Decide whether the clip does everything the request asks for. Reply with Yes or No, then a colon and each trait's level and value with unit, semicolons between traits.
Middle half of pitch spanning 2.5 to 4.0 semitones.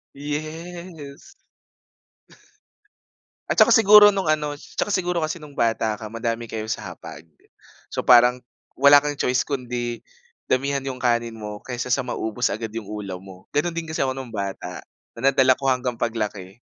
No: average, 4.5 semitones